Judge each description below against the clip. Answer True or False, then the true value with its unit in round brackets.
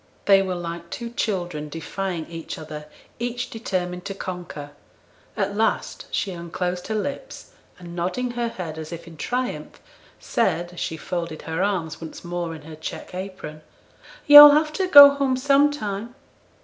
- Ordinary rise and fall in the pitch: False (6.0 semitones)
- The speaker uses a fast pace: False (160 wpm)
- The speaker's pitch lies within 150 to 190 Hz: True (185 Hz)